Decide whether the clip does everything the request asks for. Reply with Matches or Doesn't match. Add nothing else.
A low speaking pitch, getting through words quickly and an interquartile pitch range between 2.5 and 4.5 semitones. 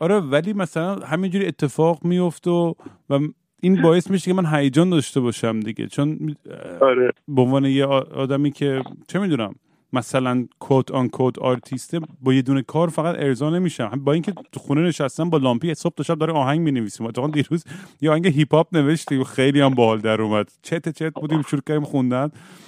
Doesn't match